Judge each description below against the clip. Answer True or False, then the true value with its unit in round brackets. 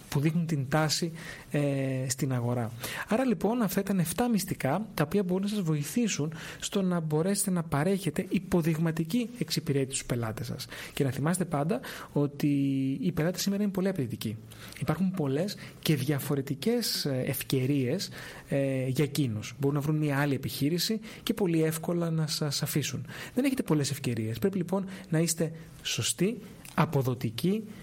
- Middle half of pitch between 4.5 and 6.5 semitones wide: True (5.2 semitones)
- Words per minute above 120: True (150 wpm)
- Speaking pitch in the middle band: True (155 Hz)